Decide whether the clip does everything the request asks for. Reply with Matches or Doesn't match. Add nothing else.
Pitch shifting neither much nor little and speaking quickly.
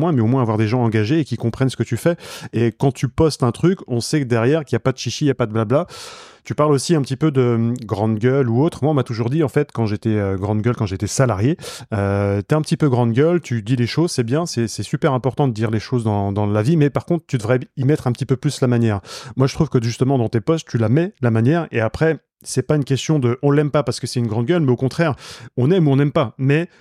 Matches